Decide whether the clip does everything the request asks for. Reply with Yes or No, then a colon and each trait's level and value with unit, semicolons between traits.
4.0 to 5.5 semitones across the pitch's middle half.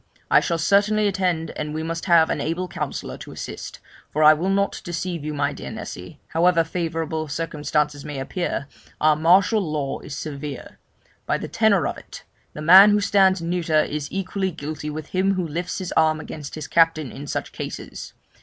No: average, 3.3 semitones